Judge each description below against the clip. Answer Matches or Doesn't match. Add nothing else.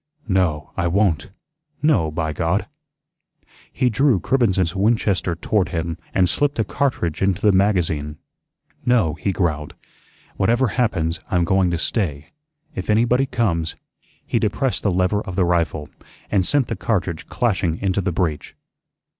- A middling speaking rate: Matches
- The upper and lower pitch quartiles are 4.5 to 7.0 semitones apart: Matches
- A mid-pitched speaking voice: Doesn't match